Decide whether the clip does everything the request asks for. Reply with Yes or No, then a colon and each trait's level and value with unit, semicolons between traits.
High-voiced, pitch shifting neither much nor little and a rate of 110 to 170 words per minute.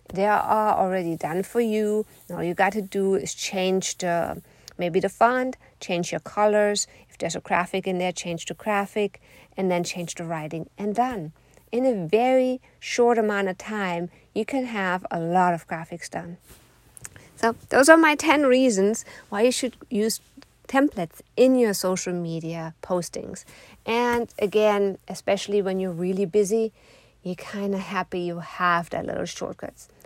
Yes: high, 200 Hz; average, 4.1 semitones; average, 160 wpm